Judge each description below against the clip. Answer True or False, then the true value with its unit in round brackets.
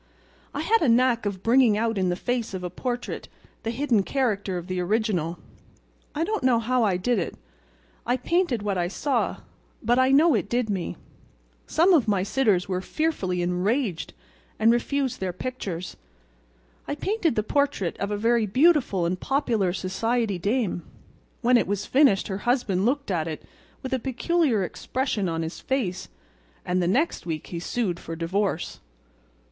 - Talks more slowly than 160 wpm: False (165 wpm)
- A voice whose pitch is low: False (220 Hz)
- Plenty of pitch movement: True (5.8 semitones)